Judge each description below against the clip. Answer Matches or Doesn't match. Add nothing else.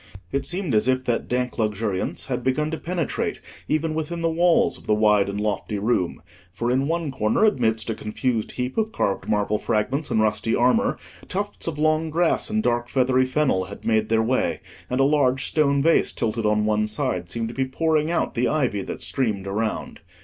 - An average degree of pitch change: Doesn't match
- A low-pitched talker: Matches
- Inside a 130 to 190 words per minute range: Doesn't match